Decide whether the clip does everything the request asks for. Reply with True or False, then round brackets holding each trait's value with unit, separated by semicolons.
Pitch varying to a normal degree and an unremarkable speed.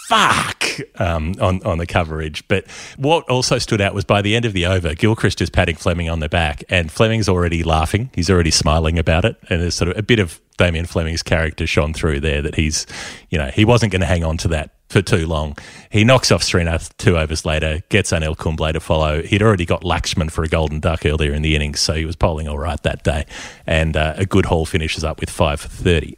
False (3.7 semitones; 240 wpm)